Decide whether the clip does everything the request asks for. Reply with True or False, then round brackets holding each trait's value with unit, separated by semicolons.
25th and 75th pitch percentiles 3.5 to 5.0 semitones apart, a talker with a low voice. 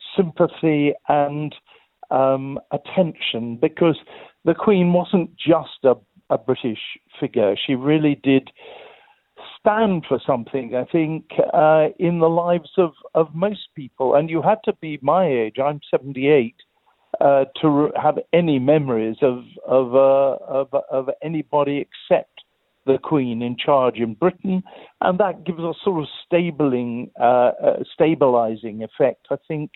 False (4.3 semitones; 150 Hz)